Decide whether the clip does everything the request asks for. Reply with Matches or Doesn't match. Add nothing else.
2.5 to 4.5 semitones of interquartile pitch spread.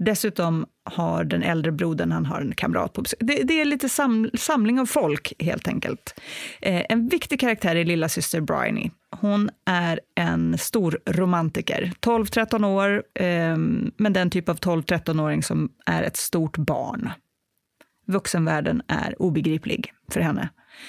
Doesn't match